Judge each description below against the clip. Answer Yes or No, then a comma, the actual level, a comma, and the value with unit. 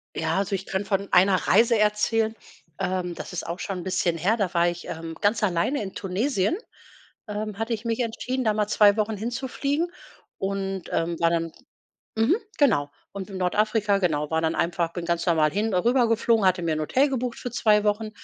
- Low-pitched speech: No, high, 200 Hz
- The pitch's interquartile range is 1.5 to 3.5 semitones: No, average, 4.3 semitones